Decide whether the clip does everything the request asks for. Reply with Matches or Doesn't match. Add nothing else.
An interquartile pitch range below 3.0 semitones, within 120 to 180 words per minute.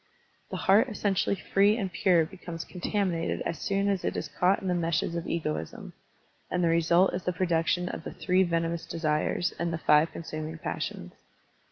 Doesn't match